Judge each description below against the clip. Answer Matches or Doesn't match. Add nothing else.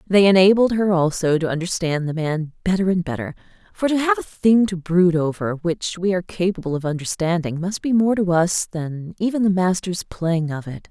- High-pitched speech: Doesn't match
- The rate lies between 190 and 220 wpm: Matches